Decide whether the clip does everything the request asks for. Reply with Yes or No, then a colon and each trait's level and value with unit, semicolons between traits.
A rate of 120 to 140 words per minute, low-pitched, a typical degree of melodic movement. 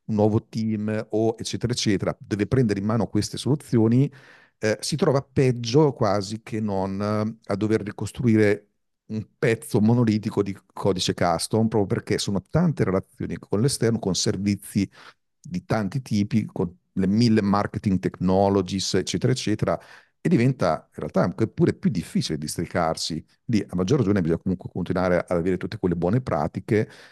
No: average, 155 wpm; low, 105 Hz; average, 3.1 semitones